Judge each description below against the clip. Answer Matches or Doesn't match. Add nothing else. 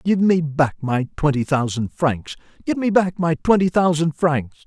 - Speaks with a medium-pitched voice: Matches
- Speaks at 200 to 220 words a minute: Doesn't match